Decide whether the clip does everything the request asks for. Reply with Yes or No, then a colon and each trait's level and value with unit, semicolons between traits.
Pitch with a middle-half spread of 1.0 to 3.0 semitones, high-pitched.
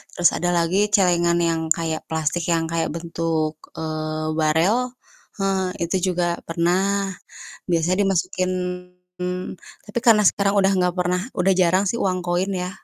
No: narrow, 2.5 semitones; medium, 175 Hz